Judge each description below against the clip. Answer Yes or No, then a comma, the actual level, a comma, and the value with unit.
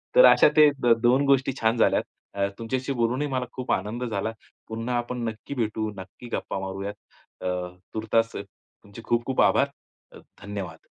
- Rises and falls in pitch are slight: No, average, 3.4 semitones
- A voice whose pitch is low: Yes, low, 115 Hz